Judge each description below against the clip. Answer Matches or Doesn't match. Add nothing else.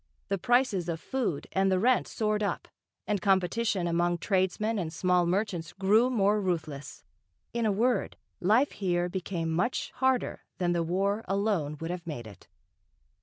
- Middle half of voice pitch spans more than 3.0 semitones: Matches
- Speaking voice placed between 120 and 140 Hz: Doesn't match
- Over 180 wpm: Doesn't match